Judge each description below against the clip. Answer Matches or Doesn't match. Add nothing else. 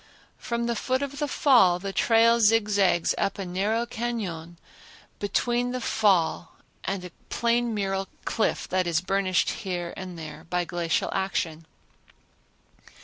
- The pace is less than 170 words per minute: Matches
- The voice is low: Doesn't match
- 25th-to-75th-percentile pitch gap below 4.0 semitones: Doesn't match